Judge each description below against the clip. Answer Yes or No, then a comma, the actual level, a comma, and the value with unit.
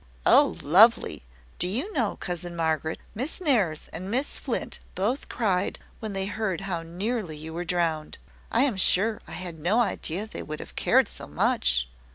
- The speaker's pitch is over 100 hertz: Yes, medium, 185 Hz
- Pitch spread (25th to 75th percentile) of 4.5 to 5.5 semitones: Yes, average, 5.2 semitones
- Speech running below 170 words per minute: No, average, 175 wpm